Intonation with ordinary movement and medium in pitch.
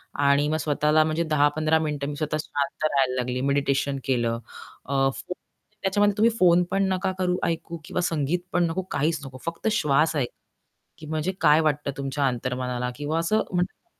Yes: average, 3.3 semitones; medium, 150 Hz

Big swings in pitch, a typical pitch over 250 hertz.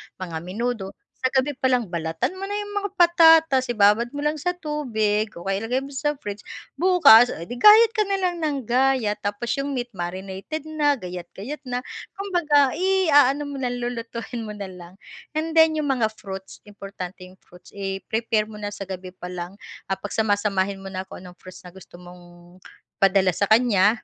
No: wide, 7.2 semitones; high, 225 Hz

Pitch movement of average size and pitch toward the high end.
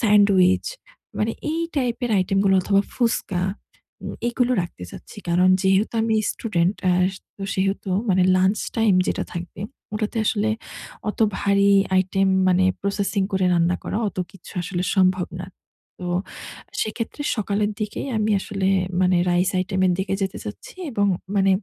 No: narrow, 2.2 semitones; high, 195 Hz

